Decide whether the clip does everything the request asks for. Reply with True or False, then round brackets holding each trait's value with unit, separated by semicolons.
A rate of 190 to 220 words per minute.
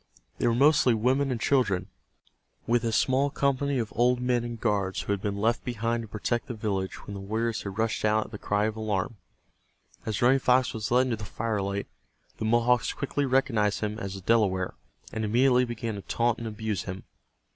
True (200 wpm)